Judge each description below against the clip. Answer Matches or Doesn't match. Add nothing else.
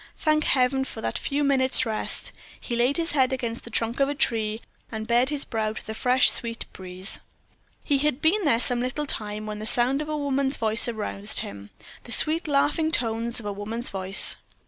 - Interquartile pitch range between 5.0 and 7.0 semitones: Doesn't match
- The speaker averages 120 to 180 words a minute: Doesn't match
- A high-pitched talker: Matches